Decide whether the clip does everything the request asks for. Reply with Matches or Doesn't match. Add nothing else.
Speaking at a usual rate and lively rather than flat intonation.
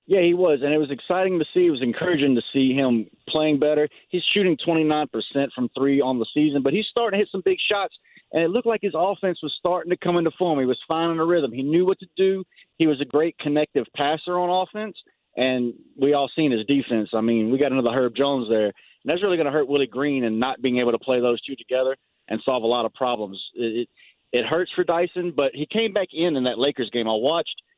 Doesn't match